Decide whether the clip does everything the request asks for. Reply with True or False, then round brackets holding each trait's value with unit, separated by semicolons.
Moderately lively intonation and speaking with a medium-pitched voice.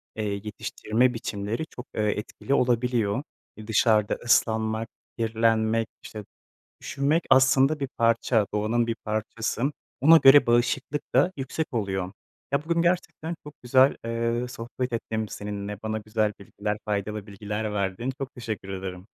False (3.4 semitones; 115 Hz)